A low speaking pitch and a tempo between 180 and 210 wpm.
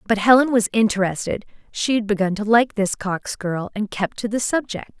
No: high, 215 Hz; fast, 205 wpm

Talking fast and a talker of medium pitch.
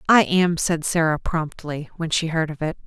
Yes: fast, 210 wpm; medium, 165 Hz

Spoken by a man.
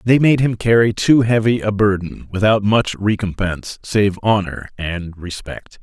Yes: male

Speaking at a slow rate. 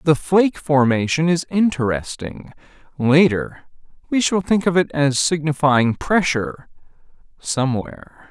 Yes: slow, 100 wpm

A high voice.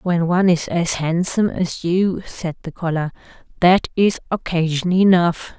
No: medium, 175 Hz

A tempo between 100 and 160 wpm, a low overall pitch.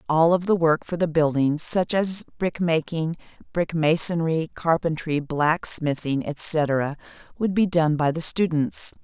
No: average, 140 wpm; medium, 160 Hz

